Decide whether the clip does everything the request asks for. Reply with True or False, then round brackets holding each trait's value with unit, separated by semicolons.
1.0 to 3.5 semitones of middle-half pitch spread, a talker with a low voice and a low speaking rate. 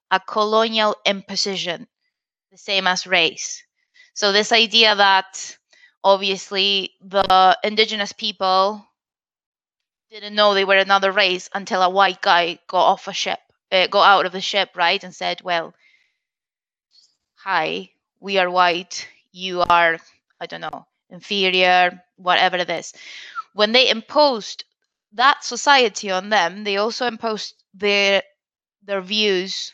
False (2.5 semitones; 195 Hz; 130 wpm)